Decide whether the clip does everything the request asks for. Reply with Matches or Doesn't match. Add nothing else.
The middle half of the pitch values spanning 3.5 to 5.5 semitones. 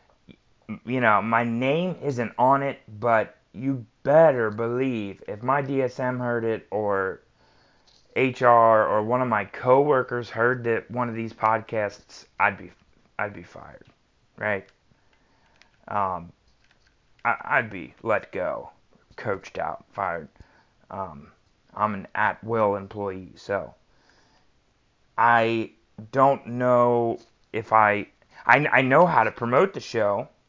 Doesn't match